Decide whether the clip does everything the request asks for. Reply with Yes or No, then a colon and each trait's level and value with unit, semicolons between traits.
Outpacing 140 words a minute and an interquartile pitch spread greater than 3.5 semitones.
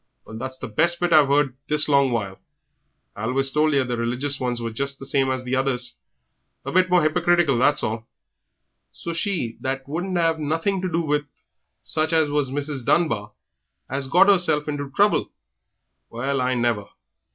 Yes: average, 185 wpm; average, 4.2 semitones